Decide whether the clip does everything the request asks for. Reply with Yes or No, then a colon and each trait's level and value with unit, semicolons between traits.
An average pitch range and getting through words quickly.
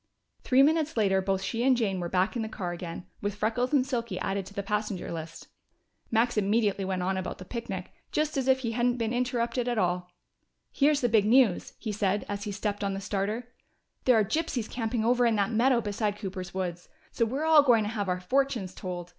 Yes: average, 4.1 semitones; fast, 220 wpm